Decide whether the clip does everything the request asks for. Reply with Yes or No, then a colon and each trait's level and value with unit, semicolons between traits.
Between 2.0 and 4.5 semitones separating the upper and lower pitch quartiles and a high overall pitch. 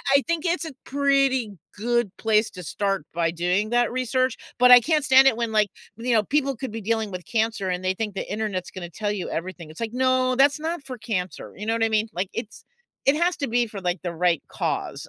No: average, 5.2 semitones; high, 225 Hz